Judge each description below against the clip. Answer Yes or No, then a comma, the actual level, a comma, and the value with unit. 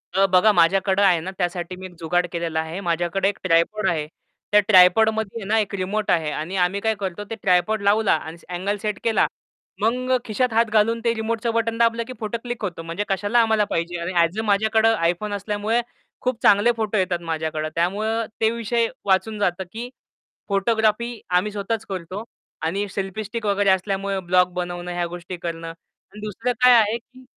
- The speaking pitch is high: Yes, high, 200 Hz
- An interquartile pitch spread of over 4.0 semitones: No, average, 3.7 semitones